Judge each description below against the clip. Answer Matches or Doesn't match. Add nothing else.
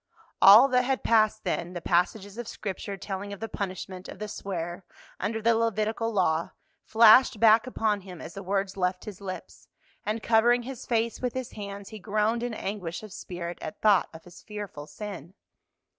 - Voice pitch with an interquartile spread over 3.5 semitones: Doesn't match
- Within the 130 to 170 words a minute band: Doesn't match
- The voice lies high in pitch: Matches